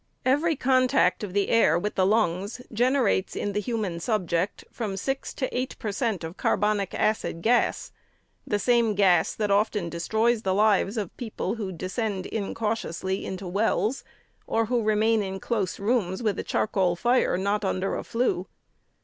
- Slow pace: No, average, 165 wpm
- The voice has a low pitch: No, high, 210 Hz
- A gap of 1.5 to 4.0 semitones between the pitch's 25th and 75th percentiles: Yes, average, 3.3 semitones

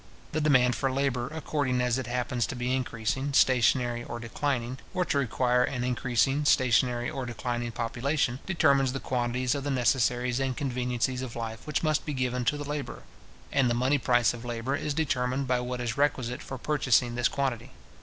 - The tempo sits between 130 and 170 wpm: No, average, 185 wpm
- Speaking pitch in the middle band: No, low, 125 Hz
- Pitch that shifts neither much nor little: No, narrow, 2.1 semitones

